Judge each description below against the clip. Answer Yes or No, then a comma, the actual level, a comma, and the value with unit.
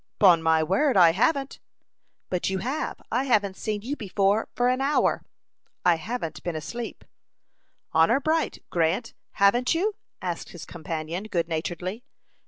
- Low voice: No, high, 195 Hz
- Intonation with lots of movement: Yes, wide, 6.5 semitones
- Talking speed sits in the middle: Yes, average, 145 wpm